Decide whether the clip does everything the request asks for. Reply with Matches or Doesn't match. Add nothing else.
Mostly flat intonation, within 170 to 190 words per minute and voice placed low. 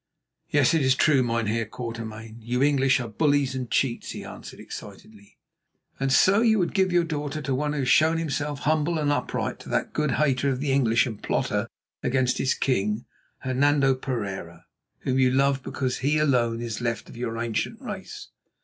Doesn't match